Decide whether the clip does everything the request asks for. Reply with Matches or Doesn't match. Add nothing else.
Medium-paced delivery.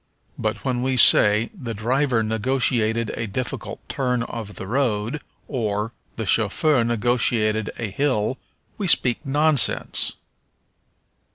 Doesn't match